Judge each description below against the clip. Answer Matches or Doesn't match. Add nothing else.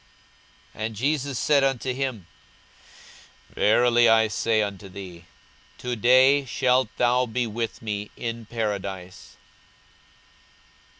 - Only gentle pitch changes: Doesn't match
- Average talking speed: Doesn't match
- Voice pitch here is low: Matches